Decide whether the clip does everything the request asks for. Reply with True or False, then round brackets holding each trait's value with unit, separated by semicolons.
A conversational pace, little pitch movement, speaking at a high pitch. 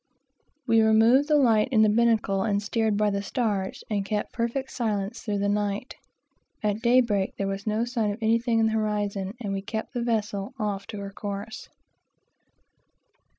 True (175 wpm; 2.3 semitones; 215 Hz)